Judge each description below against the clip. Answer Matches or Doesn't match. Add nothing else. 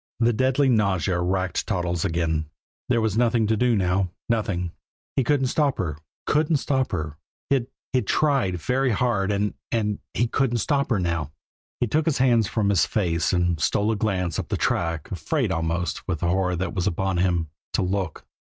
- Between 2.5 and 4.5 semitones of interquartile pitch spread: Doesn't match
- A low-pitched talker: Matches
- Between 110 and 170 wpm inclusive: Doesn't match